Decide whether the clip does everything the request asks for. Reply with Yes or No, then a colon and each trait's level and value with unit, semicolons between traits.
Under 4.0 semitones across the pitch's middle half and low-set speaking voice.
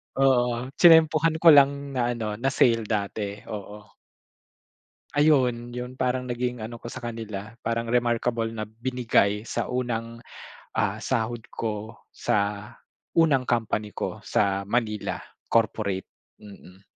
Yes: average, 2.9 semitones; low, 115 Hz